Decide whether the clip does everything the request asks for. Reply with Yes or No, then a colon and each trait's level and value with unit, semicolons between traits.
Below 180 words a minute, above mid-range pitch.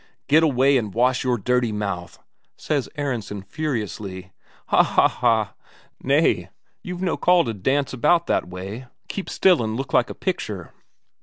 No: average, 155 wpm; low, 125 Hz